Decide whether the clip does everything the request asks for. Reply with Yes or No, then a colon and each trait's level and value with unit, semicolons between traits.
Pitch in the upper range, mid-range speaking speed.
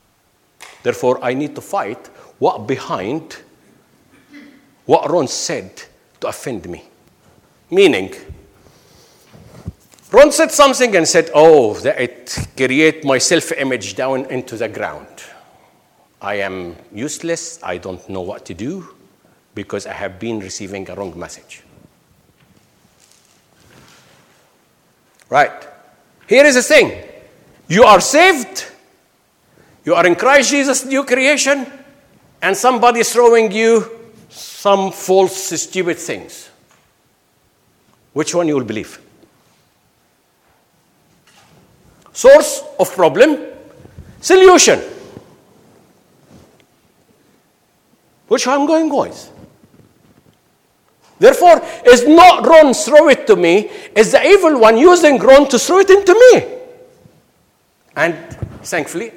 No: high, 230 Hz; slow, 110 wpm